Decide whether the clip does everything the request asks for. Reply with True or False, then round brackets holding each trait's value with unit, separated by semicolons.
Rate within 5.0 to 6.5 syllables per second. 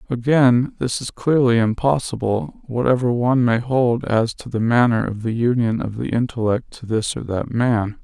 False (4.7 syllables/s)